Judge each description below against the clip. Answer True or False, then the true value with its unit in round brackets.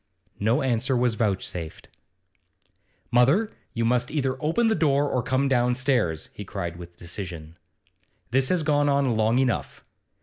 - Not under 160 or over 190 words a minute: False (140 wpm)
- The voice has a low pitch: True (125 Hz)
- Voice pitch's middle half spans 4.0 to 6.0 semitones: True (5.0 semitones)